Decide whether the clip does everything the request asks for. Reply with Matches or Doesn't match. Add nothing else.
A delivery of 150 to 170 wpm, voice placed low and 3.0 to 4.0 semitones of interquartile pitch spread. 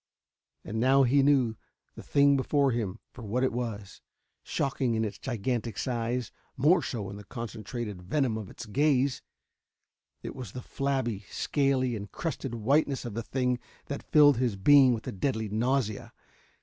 Matches